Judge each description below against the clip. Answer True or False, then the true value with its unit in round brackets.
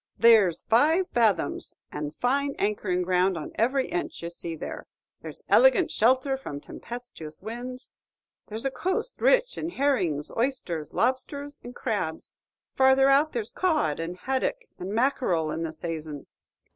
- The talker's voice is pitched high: True (235 Hz)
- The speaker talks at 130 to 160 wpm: True (145 wpm)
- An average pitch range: False (8.0 semitones)